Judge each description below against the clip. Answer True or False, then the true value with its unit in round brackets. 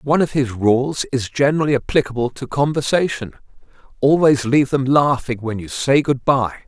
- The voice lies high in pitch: False (130 Hz)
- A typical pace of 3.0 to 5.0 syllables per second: False (5.4 syllables/s)